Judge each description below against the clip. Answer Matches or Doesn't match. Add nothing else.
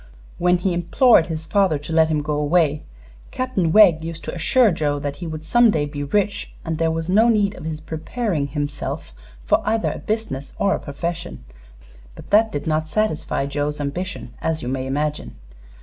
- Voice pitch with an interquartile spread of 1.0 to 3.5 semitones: Doesn't match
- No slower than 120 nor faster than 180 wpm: Doesn't match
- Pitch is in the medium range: Matches